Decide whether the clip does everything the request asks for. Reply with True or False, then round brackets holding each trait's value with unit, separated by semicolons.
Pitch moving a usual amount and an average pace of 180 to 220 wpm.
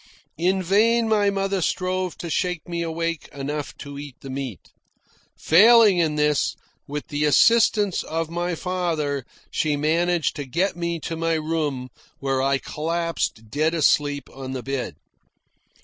False (3.7 semitones; 150 wpm)